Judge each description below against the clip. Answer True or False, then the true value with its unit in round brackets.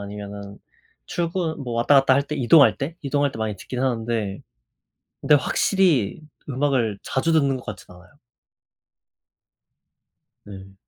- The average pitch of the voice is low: True (125 Hz)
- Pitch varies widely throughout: True (5.9 semitones)